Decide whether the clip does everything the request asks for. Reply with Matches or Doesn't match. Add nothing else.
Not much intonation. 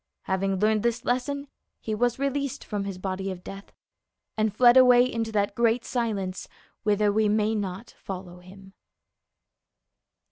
Doesn't match